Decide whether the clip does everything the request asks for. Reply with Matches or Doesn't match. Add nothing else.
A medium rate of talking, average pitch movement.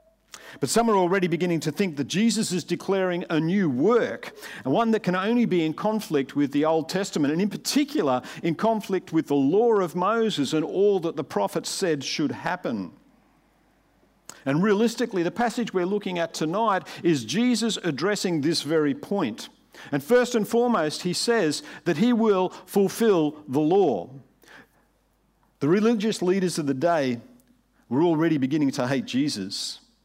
Doesn't match